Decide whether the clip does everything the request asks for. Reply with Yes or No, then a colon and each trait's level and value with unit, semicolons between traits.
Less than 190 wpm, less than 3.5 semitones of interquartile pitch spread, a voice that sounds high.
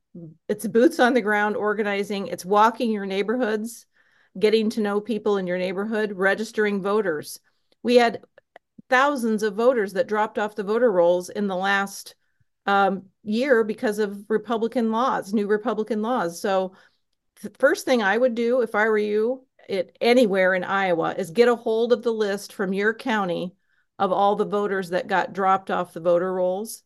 Yes: average, 175 wpm; average, 2.8 semitones; high, 215 Hz